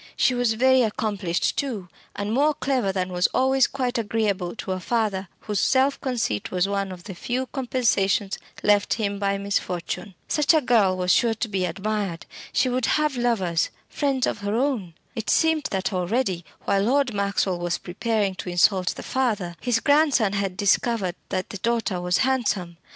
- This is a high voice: Yes, high, 210 Hz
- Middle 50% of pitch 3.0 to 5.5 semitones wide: Yes, average, 4.8 semitones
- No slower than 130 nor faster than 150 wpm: No, average, 175 wpm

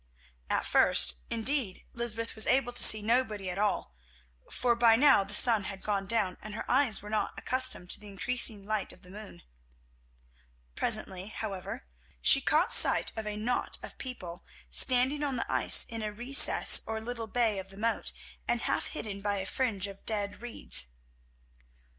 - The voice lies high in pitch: Yes, high, 215 Hz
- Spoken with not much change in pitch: No, average, 3.4 semitones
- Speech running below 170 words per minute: No, average, 175 wpm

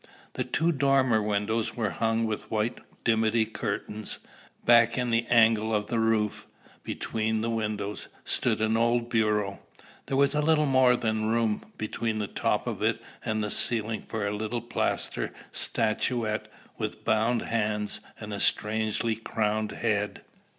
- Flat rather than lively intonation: Yes, narrow, 1.6 semitones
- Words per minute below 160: Yes, average, 150 wpm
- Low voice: Yes, low, 110 Hz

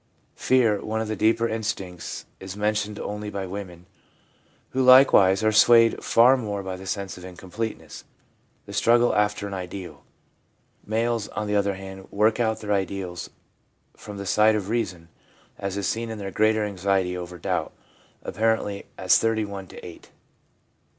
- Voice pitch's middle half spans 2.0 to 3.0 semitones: Yes, narrow, 2.5 semitones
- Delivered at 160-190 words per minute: Yes, average, 165 wpm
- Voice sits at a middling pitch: No, low, 105 Hz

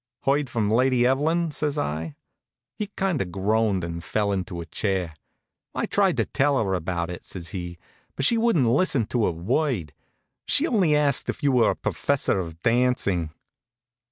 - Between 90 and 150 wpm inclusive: No, average, 175 wpm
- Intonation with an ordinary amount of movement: No, wide, 8.1 semitones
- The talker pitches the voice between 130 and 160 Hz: No, low, 115 Hz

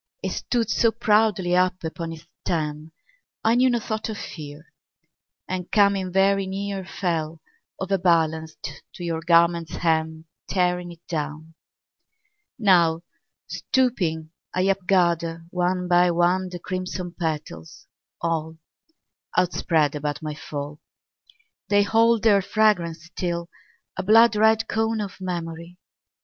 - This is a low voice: No, medium, 175 Hz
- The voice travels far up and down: No, average, 3.4 semitones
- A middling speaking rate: No, slow, 120 wpm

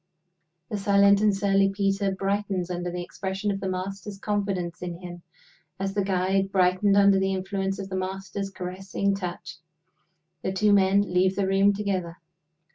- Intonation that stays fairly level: Yes, narrow, 1.3 semitones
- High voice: Yes, high, 195 Hz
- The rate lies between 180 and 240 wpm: No, average, 160 wpm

